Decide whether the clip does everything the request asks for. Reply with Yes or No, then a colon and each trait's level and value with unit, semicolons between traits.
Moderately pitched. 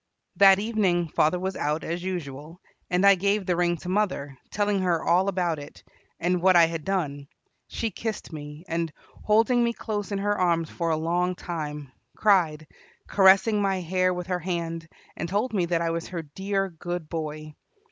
Yes: medium, 180 Hz